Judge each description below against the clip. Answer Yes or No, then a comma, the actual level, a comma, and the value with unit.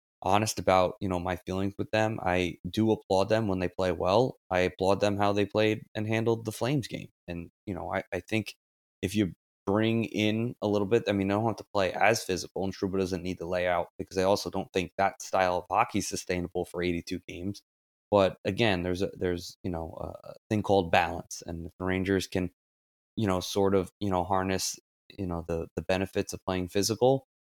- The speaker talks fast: Yes, fast, 220 wpm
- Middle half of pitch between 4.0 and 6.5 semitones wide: No, narrow, 2.5 semitones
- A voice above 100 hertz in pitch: No, very low, 95 Hz